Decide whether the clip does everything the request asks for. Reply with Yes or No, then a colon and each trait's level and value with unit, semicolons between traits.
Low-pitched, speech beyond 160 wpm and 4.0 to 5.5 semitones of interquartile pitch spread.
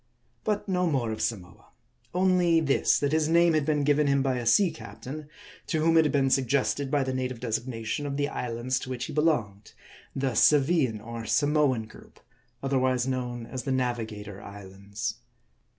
Yes: low, 130 Hz; average, 185 wpm; average, 4.4 semitones